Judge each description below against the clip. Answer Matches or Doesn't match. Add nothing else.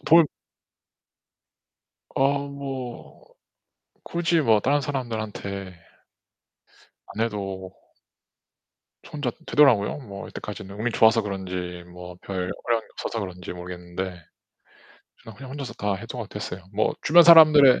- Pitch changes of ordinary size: Doesn't match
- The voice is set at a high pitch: Doesn't match